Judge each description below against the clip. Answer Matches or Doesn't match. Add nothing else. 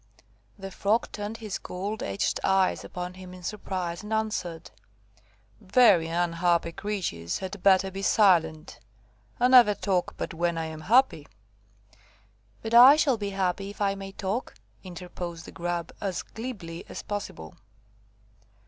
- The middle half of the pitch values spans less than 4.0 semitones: Matches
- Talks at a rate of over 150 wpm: Doesn't match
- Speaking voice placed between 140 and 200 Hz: Matches